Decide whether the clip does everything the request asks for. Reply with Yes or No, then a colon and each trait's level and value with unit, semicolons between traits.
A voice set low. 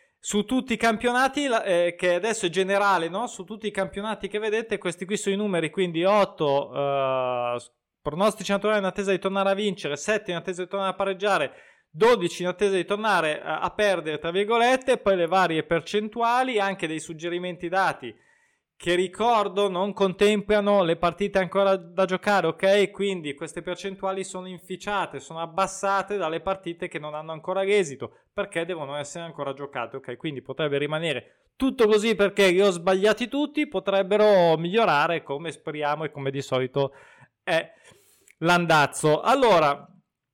No: high, 190 Hz